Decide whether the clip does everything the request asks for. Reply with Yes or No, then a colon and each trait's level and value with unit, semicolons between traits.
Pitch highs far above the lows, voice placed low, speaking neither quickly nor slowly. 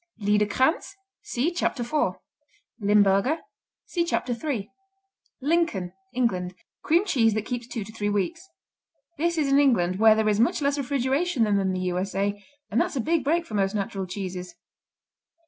No: wide, 6.1 semitones; high, 225 Hz; average, 160 wpm